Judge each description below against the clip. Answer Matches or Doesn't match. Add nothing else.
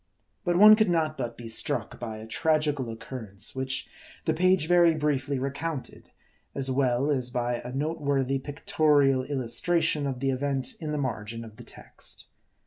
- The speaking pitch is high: Doesn't match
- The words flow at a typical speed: Matches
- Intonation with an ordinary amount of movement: Matches